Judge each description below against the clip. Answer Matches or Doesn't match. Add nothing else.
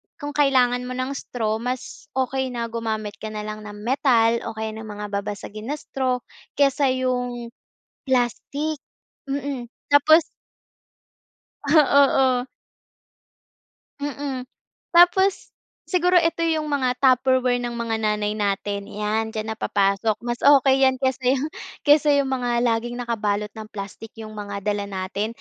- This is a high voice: Matches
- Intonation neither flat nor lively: Matches